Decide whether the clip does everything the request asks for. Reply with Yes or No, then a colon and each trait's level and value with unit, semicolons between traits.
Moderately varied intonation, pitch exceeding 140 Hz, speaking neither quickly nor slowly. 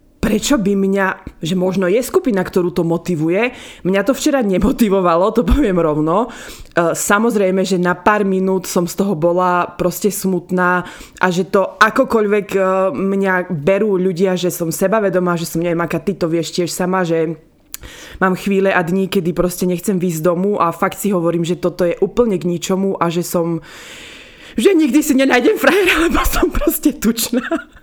No: average, 3.2 semitones; high, 190 Hz; fast, 175 wpm